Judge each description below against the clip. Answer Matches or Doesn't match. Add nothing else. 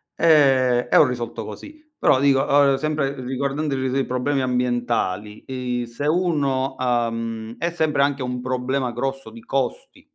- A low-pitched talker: Matches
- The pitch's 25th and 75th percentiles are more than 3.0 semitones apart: Doesn't match